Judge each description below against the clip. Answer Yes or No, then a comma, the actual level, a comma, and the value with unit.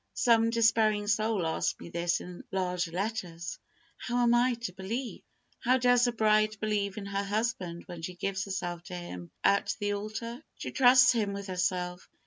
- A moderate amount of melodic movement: Yes, average, 4.1 semitones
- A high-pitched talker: Yes, high, 205 Hz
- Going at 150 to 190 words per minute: Yes, average, 175 wpm